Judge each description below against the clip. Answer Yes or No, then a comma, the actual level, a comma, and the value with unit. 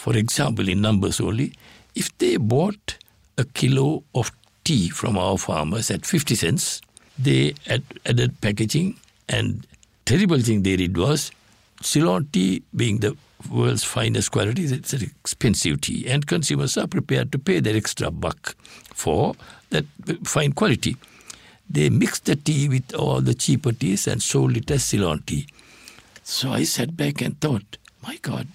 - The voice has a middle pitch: No, low, 120 Hz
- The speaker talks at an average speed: Yes, average, 160 wpm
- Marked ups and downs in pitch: Yes, wide, 6.4 semitones